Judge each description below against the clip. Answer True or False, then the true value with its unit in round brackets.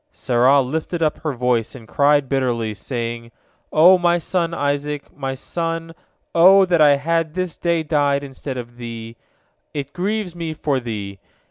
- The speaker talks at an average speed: True (160 wpm)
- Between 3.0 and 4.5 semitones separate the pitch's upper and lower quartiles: False (4.9 semitones)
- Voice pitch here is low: False (145 Hz)